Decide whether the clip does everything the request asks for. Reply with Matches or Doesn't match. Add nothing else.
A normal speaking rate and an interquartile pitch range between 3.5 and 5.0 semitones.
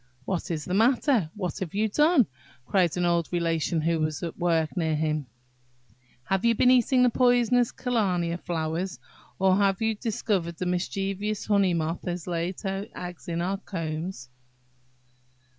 Matches